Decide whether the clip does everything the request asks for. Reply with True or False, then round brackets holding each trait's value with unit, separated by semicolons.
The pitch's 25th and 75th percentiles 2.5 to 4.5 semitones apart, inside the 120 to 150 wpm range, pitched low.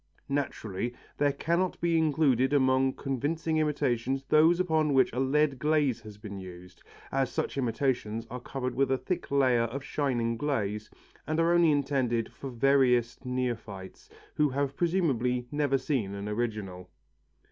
True (4.0 semitones; 145 wpm; 130 Hz)